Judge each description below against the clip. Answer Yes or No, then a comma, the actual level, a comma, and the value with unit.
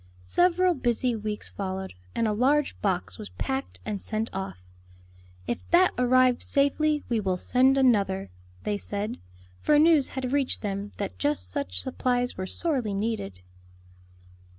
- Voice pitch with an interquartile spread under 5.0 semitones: No, wide, 5.5 semitones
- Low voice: No, high, 230 Hz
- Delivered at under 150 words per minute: Yes, average, 140 wpm